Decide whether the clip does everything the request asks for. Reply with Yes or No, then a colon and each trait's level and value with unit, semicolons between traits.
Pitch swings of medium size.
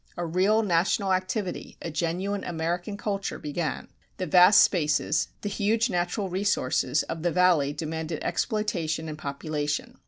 Yes: average, 3.8 semitones